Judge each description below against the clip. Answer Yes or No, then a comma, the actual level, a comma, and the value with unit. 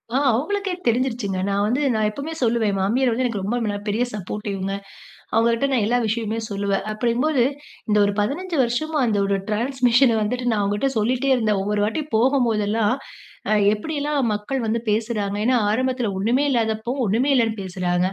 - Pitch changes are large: No, average, 3.5 semitones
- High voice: Yes, high, 225 Hz